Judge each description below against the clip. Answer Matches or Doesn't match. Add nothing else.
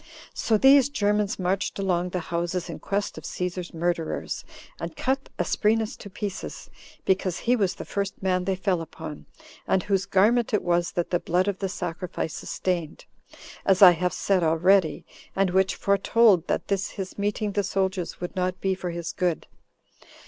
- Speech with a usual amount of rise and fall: Doesn't match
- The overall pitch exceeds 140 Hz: Matches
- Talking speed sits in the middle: Matches